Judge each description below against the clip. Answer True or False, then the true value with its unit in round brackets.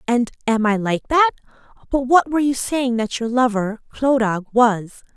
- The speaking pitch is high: True (240 Hz)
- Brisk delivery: False (165 wpm)